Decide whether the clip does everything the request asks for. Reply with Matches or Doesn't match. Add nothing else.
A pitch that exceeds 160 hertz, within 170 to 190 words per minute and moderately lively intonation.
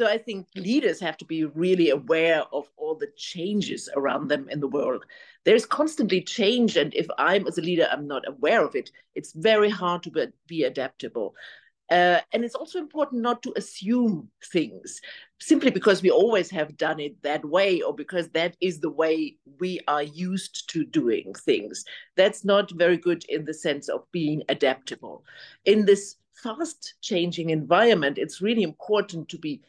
Doesn't match